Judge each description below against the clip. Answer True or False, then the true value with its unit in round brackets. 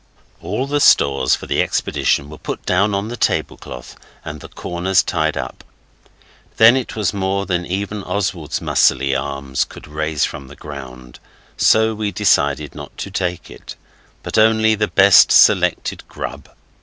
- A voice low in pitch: True (90 Hz)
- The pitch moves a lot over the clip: True (6.5 semitones)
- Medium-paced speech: True (155 wpm)